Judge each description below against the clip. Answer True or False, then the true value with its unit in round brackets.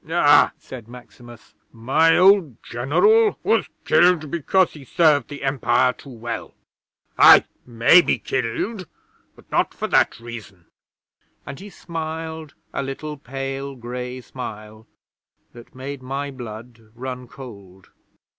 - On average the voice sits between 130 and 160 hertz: True (135 Hz)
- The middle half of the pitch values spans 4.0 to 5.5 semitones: True (4.7 semitones)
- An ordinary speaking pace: False (125 wpm)